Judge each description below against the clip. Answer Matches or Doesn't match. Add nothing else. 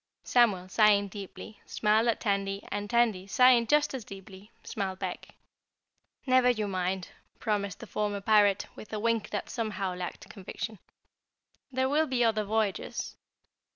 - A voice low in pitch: Doesn't match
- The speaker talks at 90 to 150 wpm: Matches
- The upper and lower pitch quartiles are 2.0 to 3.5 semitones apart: Matches